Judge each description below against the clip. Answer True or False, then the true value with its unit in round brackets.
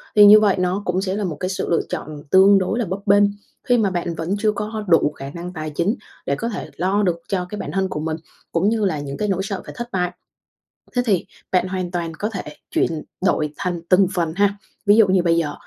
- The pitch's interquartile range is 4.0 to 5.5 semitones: False (3.3 semitones)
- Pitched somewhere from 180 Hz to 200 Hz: True (185 Hz)